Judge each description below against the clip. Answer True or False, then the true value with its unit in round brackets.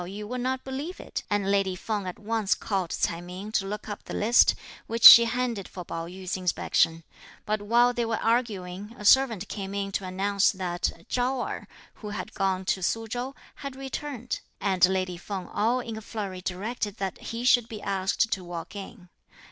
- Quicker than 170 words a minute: True (195 wpm)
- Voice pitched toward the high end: True (205 Hz)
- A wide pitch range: False (3.8 semitones)